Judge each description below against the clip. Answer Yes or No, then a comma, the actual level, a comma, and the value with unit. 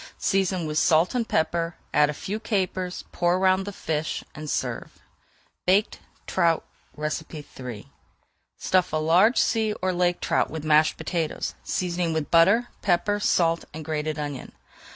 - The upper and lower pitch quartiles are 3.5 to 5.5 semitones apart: No, average, 3.1 semitones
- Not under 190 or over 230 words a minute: No, average, 145 wpm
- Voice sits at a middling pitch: Yes, medium, 170 Hz